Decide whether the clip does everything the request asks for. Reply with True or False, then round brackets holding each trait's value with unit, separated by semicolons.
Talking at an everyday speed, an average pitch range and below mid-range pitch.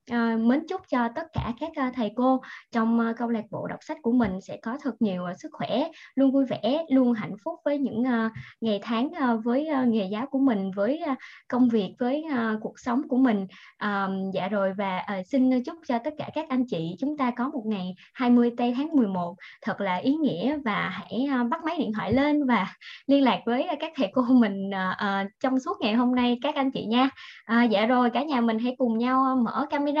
False (205 wpm; 3.8 semitones; 245 Hz)